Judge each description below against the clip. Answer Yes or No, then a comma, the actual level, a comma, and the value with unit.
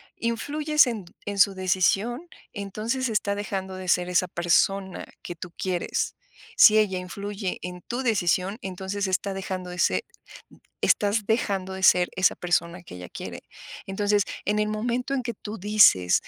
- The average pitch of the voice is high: Yes, high, 195 Hz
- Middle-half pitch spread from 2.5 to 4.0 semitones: Yes, average, 2.8 semitones